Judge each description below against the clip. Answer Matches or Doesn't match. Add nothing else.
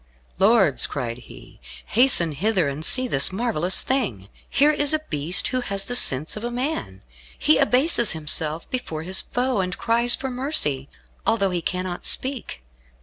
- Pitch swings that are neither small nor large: Doesn't match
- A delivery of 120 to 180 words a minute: Matches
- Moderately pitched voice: Doesn't match